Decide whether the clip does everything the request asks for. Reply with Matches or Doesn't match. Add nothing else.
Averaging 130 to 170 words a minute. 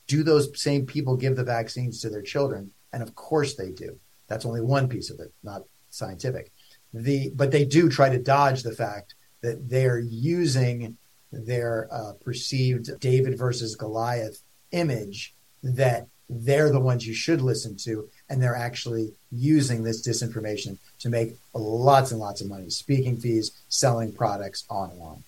Matches